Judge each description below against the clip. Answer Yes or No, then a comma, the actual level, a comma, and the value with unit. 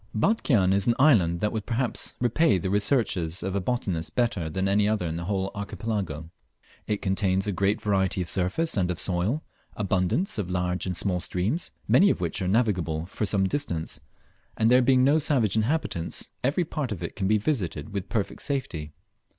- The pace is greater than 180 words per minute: Yes, average, 190 wpm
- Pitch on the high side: No, low, 100 Hz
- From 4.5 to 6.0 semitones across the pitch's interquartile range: Yes, average, 4.9 semitones